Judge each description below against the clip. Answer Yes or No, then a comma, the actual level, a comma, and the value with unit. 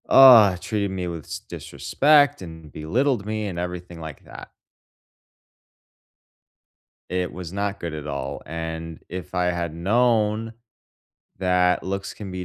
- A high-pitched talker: No, very low, 90 Hz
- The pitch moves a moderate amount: Yes, average, 4.2 semitones